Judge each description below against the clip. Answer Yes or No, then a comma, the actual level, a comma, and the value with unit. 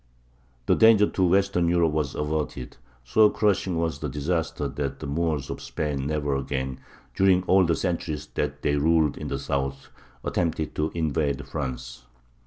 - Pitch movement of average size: Yes, average, 3.6 semitones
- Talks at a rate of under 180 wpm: Yes, average, 160 wpm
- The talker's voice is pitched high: No, very low, 75 Hz